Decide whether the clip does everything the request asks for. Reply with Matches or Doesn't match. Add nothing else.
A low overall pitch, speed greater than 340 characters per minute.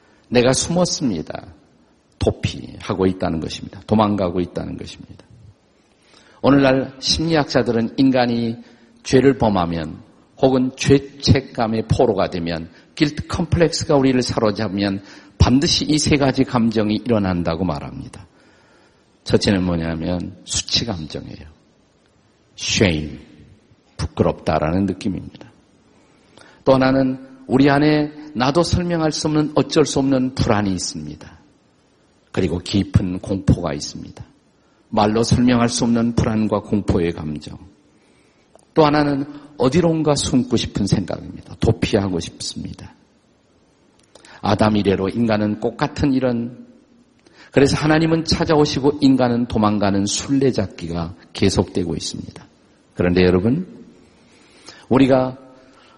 Doesn't match